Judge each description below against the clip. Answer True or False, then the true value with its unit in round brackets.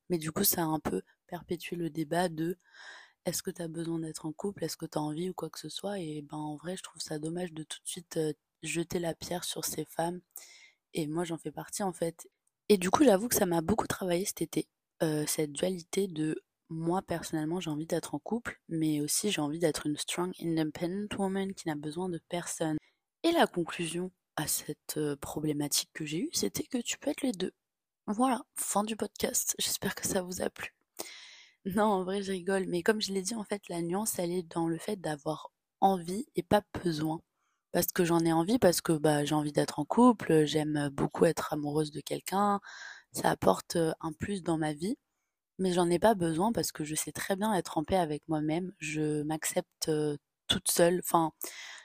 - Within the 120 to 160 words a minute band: False (215 wpm)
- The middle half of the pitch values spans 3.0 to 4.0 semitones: True (3.7 semitones)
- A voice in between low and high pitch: True (170 Hz)